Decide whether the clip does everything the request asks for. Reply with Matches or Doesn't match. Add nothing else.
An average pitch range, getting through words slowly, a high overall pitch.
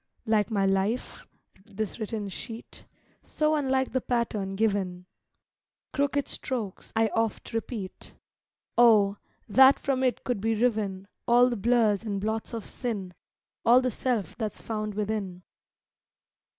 Matches